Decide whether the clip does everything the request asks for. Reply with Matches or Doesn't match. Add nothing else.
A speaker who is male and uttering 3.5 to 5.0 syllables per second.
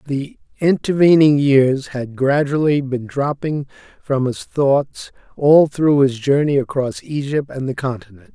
Matches